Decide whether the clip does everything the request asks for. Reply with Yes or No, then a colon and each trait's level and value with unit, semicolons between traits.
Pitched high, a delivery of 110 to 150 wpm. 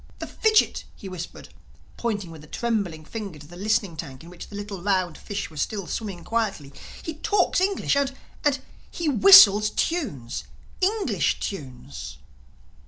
Yes: high, 205 Hz; average, 145 wpm